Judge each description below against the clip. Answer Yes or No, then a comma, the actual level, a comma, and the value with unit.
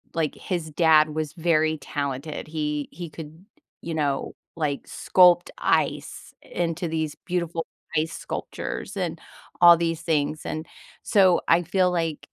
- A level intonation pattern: Yes, narrow, 2.0 semitones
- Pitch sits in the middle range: Yes, medium, 160 Hz